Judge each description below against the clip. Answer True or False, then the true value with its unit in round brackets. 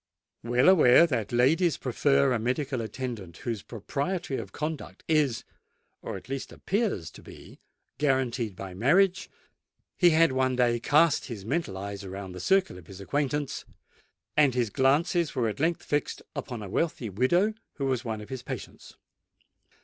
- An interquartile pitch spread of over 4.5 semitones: True (5.1 semitones)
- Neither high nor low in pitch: False (130 Hz)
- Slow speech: False (155 wpm)